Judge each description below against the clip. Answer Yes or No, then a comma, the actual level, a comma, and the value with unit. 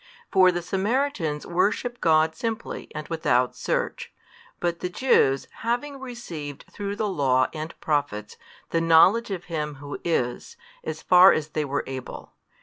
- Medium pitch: Yes, medium, 165 Hz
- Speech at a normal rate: Yes, average, 145 wpm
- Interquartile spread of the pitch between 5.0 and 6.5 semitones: Yes, wide, 5.6 semitones